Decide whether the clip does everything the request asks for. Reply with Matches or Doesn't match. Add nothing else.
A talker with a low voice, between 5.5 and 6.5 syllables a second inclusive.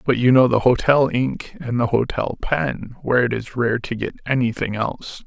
Doesn't match